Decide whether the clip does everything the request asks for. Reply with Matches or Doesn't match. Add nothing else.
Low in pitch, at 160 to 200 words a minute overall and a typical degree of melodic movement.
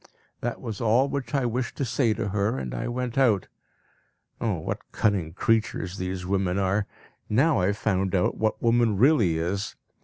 Matches